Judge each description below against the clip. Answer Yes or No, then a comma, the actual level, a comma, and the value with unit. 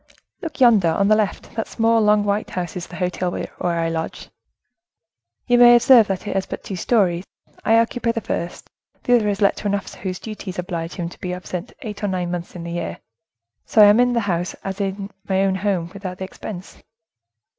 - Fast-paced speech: Yes, fast, 215 wpm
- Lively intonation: No, average, 3.2 semitones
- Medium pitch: No, high, 195 Hz